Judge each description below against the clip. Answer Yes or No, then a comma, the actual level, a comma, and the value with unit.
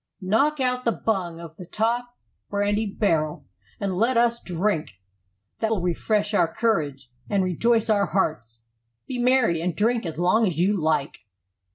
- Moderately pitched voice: No, high, 205 Hz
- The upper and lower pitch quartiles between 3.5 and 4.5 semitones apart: No, average, 5.2 semitones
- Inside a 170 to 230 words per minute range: No, average, 160 wpm